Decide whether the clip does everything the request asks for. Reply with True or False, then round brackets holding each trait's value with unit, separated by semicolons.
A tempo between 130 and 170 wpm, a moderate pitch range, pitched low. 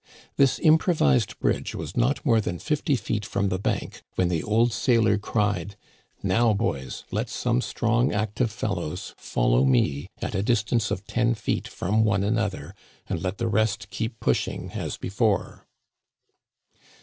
True (155 wpm; 3.8 semitones; 105 Hz)